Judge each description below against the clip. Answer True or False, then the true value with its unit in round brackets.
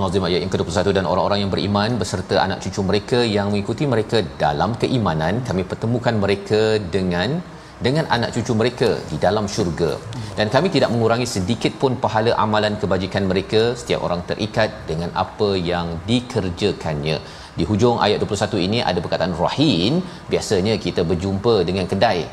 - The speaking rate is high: True (155 wpm)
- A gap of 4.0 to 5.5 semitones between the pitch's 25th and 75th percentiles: False (3.5 semitones)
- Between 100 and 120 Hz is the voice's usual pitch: True (105 Hz)